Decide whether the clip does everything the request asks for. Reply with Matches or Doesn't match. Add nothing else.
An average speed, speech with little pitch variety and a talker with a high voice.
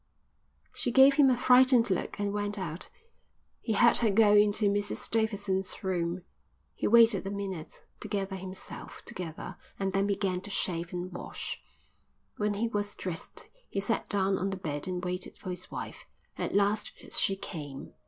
Matches